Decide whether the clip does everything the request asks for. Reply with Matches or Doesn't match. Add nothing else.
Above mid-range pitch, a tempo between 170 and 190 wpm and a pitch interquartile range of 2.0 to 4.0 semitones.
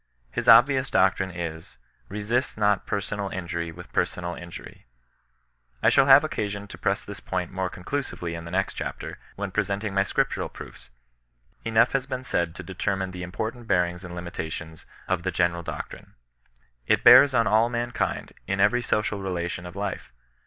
Doesn't match